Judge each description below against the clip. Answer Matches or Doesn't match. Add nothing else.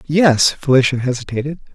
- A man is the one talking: Matches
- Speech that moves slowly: Matches